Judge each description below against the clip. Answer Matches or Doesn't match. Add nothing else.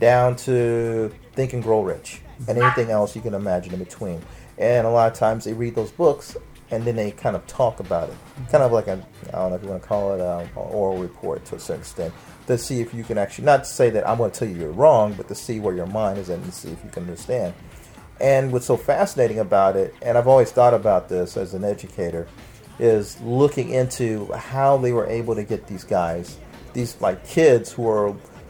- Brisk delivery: Matches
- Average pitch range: Matches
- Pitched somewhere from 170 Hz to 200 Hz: Doesn't match